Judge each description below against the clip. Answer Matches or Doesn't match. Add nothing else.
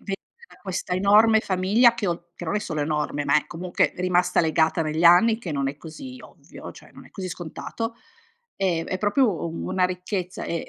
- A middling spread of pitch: Matches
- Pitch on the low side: Doesn't match